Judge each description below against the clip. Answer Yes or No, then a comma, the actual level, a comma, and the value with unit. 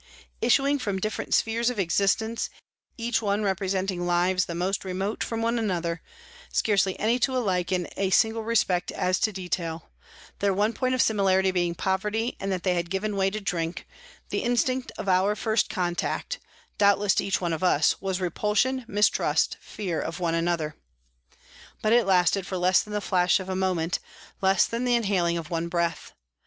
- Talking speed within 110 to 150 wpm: No, average, 180 wpm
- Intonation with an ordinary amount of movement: Yes, average, 3.4 semitones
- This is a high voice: Yes, high, 195 Hz